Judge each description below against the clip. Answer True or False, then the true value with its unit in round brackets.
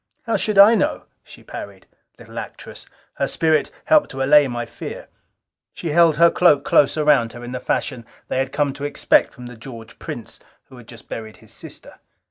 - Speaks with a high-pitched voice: False (140 Hz)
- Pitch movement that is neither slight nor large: True (5.0 semitones)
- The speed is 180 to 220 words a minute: True (195 wpm)